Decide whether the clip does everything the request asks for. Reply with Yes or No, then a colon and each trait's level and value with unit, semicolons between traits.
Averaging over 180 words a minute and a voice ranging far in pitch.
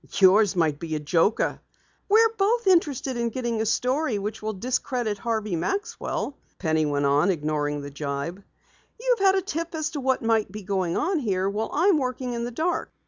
Yes: average, 190 wpm; wide, 8.9 semitones